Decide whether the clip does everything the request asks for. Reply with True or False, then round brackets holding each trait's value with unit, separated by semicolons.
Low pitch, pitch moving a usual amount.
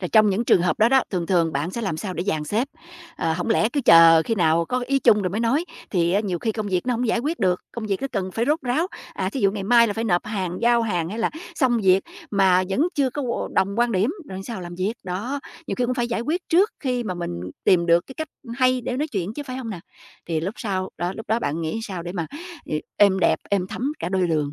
False (205 Hz; 5.0 semitones)